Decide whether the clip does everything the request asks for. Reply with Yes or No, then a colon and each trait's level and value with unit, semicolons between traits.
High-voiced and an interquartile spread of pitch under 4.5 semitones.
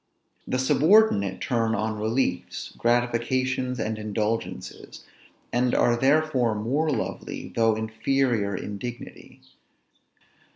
No: low, 120 Hz; average, 3.0 semitones